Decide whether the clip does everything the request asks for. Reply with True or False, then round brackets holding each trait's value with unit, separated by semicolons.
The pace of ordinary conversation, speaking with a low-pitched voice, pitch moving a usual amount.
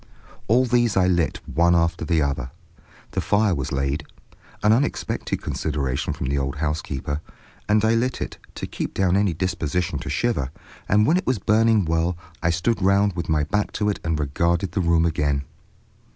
False (175 wpm; 85 Hz; 5.7 semitones)